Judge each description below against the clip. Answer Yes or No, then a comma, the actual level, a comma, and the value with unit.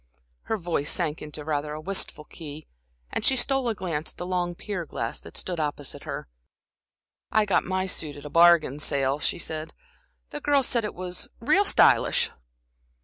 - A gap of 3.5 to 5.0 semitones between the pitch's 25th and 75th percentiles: Yes, average, 4.7 semitones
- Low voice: No, medium, 170 Hz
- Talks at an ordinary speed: Yes, average, 180 wpm